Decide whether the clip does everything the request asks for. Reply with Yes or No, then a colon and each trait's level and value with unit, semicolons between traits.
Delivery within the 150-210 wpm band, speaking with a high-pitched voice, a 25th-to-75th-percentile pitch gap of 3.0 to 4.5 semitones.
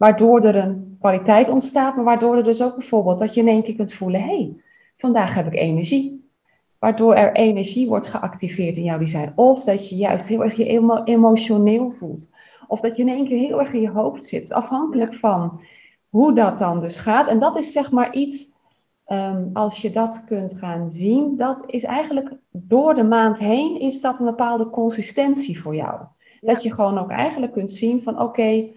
Yes: fast, 200 wpm; high, 225 Hz; average, 3.9 semitones